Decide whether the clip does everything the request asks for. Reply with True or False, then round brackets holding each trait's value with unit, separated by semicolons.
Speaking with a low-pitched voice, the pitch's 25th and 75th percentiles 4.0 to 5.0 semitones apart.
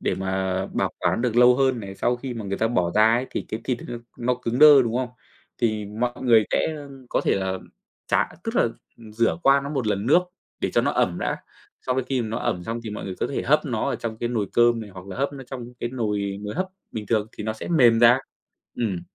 False (115 Hz; 3.3 semitones)